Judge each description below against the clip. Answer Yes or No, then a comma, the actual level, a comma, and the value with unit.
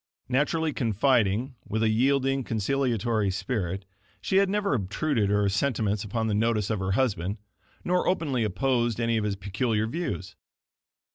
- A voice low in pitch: Yes, low, 115 Hz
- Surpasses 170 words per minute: No, average, 145 wpm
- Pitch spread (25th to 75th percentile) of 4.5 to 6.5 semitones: Yes, average, 4.8 semitones